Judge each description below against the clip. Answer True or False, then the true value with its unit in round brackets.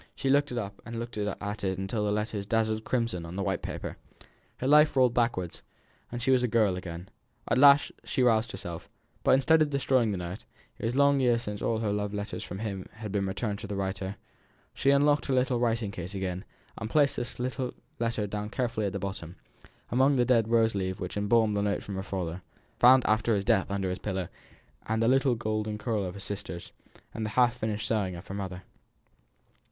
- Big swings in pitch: False (3.7 semitones)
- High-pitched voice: False (110 Hz)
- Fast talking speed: True (210 wpm)